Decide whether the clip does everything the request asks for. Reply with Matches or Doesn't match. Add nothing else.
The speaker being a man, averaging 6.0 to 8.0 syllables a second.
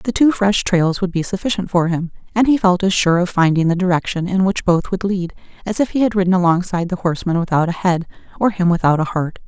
Doesn't match